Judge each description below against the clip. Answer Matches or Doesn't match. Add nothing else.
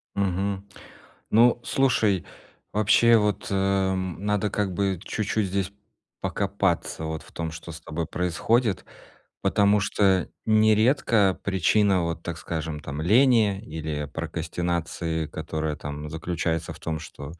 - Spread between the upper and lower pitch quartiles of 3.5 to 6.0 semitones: Matches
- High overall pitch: Doesn't match